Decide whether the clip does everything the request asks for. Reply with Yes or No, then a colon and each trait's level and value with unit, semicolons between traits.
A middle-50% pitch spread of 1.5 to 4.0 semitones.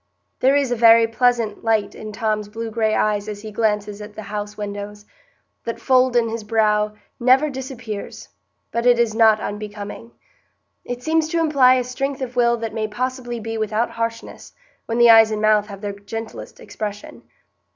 Yes: narrow, 2.4 semitones